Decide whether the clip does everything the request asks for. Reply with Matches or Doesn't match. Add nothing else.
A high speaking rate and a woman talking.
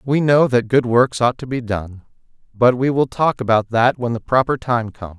Doesn't match